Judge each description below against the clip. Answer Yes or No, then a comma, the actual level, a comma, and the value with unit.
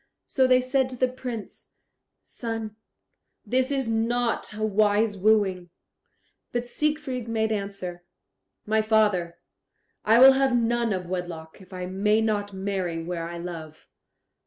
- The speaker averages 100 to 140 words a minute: Yes, slow, 135 wpm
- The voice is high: Yes, high, 215 Hz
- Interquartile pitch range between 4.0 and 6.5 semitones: Yes, average, 4.5 semitones